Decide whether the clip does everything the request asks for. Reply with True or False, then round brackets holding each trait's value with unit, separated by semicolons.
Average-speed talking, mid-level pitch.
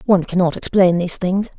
True (190 wpm; 180 Hz)